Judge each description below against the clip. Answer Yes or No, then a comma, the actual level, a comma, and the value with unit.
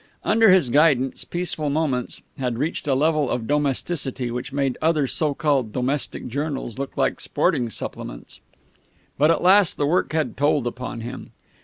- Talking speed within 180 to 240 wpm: No, average, 160 wpm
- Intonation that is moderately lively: Yes, average, 3.7 semitones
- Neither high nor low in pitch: Yes, medium, 145 Hz